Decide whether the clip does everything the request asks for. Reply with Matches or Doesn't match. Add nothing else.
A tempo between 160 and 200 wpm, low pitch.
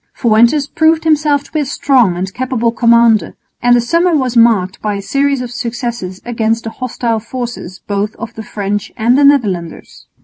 Doesn't match